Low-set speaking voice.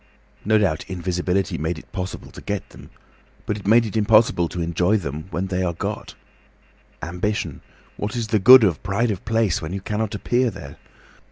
Yes: very low, 95 Hz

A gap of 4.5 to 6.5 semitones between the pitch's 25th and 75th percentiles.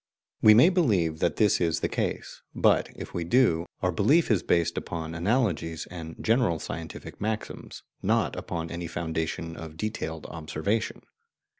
Yes: average, 4.8 semitones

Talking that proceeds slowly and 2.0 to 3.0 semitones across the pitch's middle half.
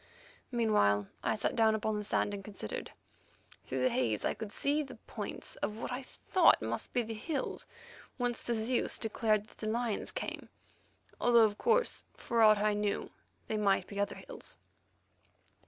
No: average, 170 wpm; average, 2.7 semitones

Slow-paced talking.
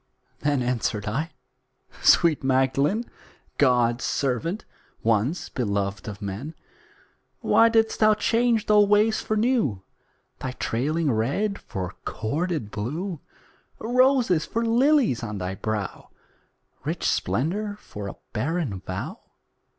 Yes: slow, 110 wpm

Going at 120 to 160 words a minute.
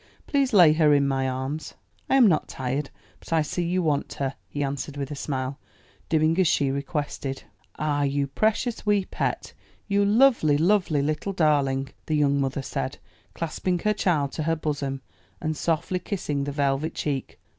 No: average, 175 wpm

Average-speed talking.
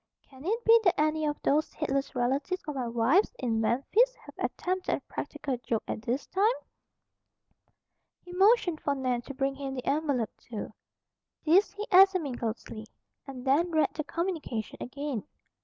Yes: average, 160 wpm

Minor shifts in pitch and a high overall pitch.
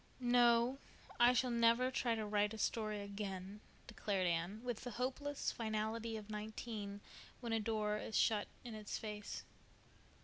Yes: narrow, 2.3 semitones; high, 220 Hz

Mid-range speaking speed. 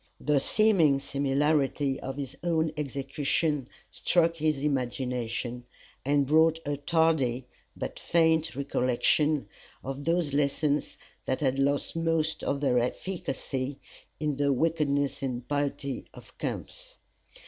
No: slow, 115 wpm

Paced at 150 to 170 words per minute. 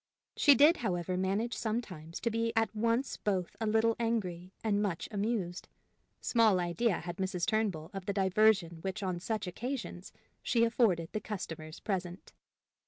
Yes: average, 155 wpm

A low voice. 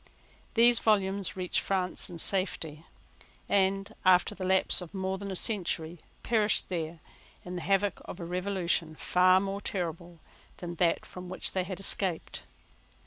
No: medium, 185 Hz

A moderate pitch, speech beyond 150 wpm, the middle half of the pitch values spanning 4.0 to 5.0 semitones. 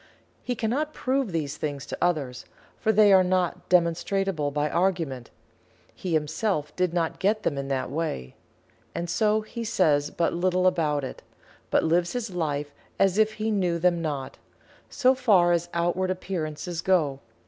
Yes: medium, 175 Hz; average, 160 wpm; average, 4.4 semitones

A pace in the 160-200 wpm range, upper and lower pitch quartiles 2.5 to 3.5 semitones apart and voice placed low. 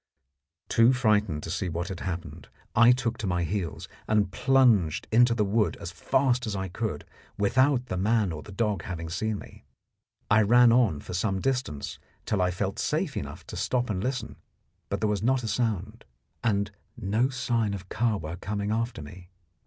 No: average, 180 wpm; average, 4.3 semitones; low, 105 Hz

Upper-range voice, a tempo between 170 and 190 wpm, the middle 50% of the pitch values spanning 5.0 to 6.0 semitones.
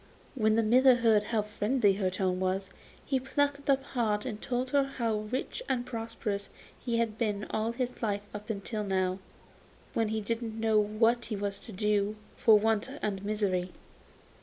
No: high, 215 Hz; average, 175 wpm; average, 2.7 semitones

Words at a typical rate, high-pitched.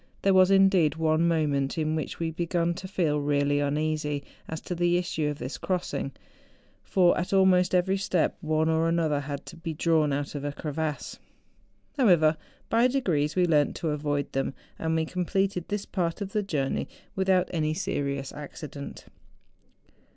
No: average, 170 wpm; medium, 160 Hz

